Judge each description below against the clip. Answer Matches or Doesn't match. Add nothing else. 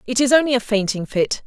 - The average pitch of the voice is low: Doesn't match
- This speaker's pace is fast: Matches